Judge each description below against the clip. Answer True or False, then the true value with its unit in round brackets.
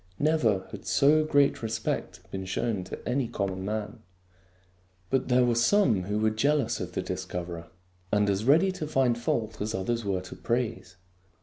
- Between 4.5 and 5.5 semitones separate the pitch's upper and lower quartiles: True (5.1 semitones)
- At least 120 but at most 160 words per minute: False (175 wpm)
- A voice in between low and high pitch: False (115 Hz)